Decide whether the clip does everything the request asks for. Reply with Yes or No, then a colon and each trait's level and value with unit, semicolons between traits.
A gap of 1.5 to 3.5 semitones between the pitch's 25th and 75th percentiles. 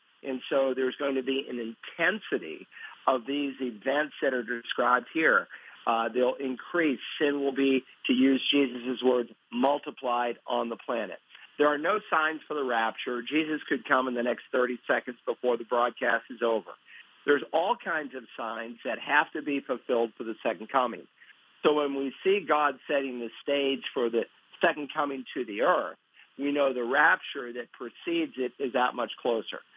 Yes: average, 2.9 semitones